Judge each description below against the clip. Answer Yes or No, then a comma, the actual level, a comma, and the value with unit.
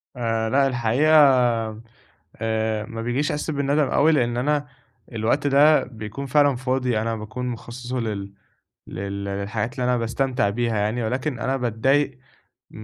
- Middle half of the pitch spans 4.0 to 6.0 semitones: No, average, 3.5 semitones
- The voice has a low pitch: Yes, low, 120 Hz